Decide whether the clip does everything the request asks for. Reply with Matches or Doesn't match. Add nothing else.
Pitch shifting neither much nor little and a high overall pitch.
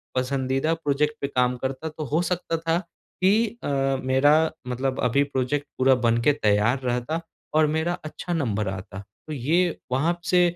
Doesn't match